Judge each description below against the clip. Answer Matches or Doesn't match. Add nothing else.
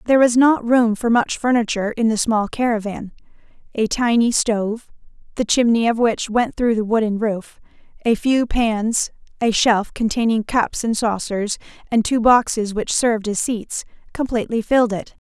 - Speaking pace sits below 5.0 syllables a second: Matches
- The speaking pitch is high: Matches